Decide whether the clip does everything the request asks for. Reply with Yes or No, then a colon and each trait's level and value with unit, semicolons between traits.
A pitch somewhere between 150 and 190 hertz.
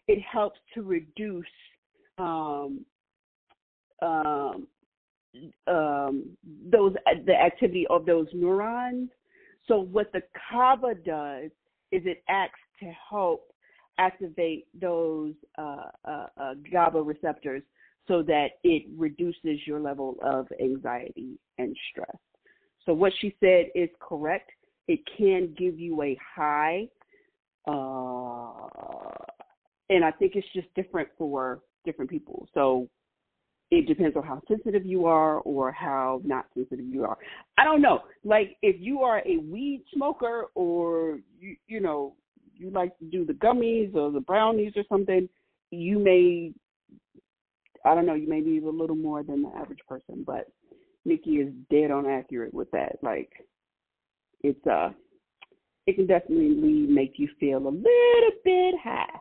Yes: medium, 185 Hz